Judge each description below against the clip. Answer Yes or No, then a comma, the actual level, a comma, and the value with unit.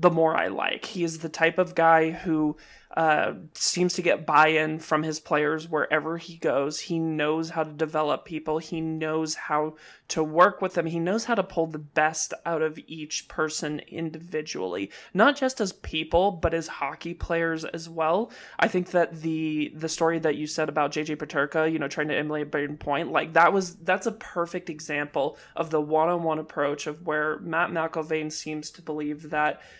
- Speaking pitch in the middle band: Yes, medium, 160 Hz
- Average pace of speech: Yes, average, 190 wpm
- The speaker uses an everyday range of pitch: No, narrow, 1.6 semitones